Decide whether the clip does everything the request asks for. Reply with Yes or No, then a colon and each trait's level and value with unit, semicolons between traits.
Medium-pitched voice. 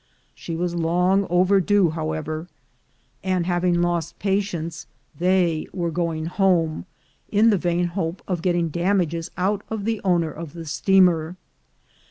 Yes: medium, 175 Hz